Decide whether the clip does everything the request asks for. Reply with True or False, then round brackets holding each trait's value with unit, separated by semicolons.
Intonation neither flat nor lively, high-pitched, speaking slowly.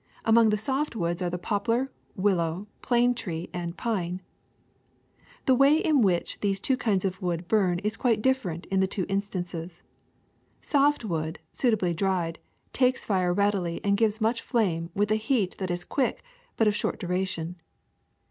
False (4.4 semitones; 195 Hz; 165 wpm)